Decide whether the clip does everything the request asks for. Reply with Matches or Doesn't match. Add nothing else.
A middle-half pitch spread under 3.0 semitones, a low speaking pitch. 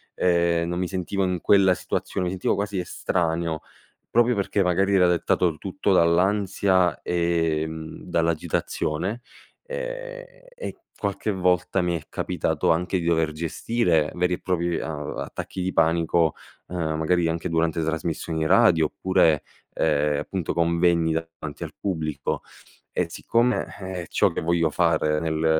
Matches